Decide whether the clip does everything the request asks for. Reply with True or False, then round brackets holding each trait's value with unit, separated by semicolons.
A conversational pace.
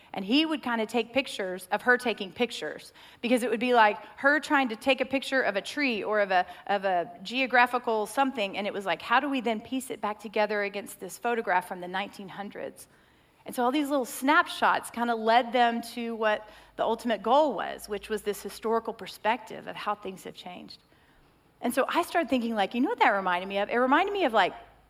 False (225 wpm)